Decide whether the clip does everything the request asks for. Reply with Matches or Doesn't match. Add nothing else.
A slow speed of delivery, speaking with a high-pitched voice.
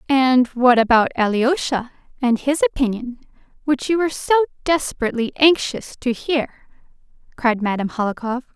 Matches